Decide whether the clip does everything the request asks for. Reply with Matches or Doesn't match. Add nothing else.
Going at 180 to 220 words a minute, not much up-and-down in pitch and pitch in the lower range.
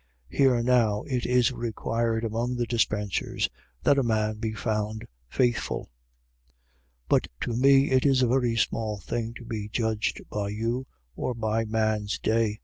Doesn't match